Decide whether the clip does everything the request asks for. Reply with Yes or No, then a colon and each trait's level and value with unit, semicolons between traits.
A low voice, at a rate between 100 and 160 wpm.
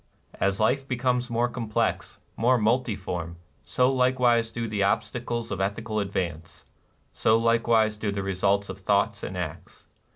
Yes: low, 115 Hz; average, 155 wpm